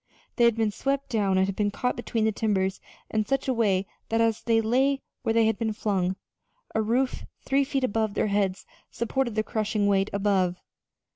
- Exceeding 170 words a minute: Yes, average, 200 wpm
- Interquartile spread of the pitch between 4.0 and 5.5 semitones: No, average, 2.7 semitones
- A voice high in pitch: Yes, high, 220 Hz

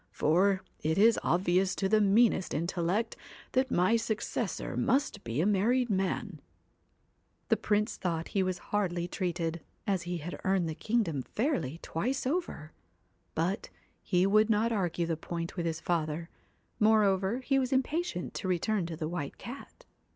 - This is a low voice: No, high, 190 Hz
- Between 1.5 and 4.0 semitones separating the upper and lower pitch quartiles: No, average, 4.4 semitones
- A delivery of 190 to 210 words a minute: No, average, 160 wpm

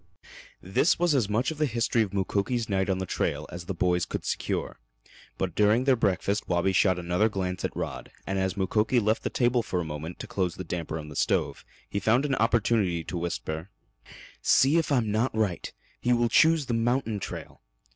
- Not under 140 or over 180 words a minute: No, fast, 205 wpm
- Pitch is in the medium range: No, low, 105 Hz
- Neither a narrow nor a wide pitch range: Yes, average, 4.7 semitones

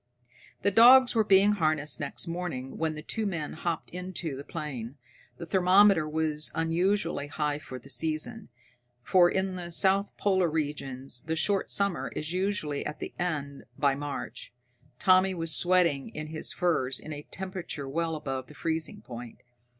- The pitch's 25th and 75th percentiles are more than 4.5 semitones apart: No, average, 4.2 semitones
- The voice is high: No, medium, 160 Hz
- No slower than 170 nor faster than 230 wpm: No, average, 160 wpm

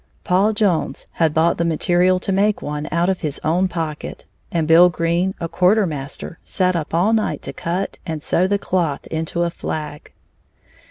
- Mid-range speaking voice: Yes, medium, 170 Hz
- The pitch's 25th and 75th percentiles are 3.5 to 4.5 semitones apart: No, narrow, 2.6 semitones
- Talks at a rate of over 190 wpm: No, average, 180 wpm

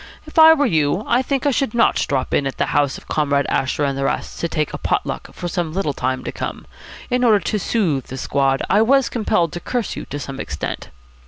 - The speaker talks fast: Yes, fast, 240 wpm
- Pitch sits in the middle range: Yes, medium, 170 Hz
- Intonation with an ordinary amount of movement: No, wide, 9.0 semitones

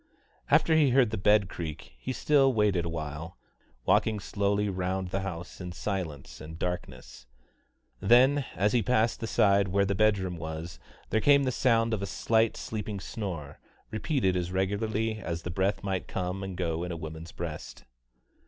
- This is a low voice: Yes, very low, 95 Hz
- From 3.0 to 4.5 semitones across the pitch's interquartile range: Yes, average, 4.0 semitones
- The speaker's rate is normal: Yes, average, 170 wpm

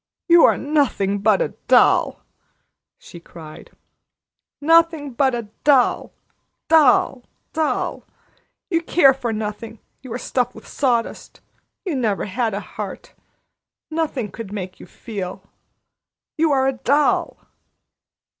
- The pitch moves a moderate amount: No, wide, 5.7 semitones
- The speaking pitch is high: Yes, very high, 250 Hz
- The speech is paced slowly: Yes, slow, 125 wpm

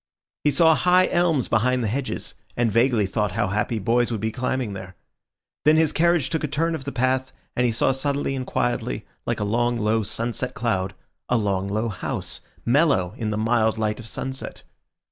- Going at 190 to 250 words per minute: Yes, average, 195 wpm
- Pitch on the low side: Yes, low, 120 Hz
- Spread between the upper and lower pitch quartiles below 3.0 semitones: No, average, 4.0 semitones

